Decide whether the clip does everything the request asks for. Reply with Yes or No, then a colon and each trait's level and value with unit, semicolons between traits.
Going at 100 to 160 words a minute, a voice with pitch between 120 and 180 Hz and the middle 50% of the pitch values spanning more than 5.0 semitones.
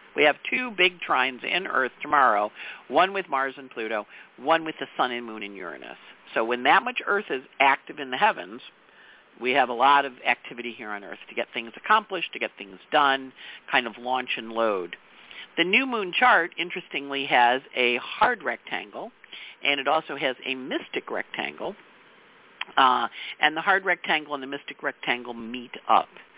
No: average, 180 wpm; low, 135 Hz; wide, 5.6 semitones